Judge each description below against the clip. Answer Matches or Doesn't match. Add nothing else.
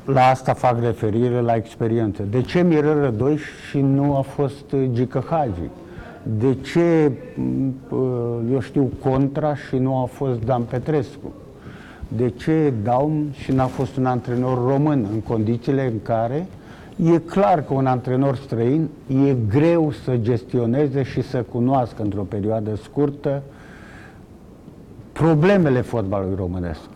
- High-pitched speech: Doesn't match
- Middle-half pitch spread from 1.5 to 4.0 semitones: Matches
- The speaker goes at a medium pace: Matches